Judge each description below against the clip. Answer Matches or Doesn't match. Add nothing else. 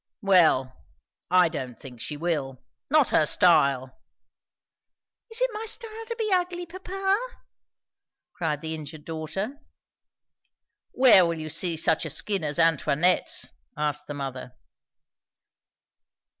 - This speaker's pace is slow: Matches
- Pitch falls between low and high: Matches